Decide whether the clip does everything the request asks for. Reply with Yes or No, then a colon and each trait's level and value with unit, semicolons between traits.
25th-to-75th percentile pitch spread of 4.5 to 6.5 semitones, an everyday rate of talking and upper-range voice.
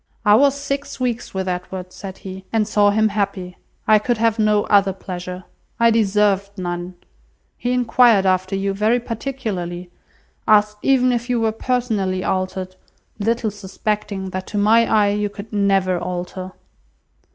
No: average, 3.2 semitones; average, 150 wpm; high, 205 Hz